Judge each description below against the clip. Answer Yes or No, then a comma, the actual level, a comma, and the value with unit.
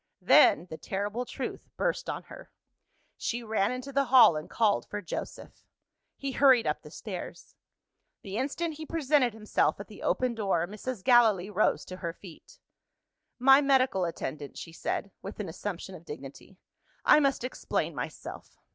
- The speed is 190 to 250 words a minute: No, average, 160 wpm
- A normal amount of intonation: No, wide, 5.8 semitones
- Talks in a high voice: Yes, high, 220 Hz